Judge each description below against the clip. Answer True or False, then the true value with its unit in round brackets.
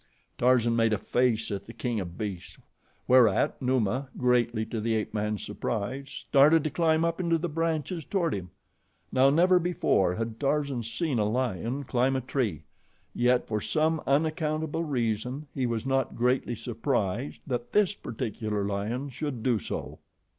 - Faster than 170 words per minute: False (160 wpm)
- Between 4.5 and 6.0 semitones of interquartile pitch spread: True (4.9 semitones)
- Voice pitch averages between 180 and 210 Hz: False (125 Hz)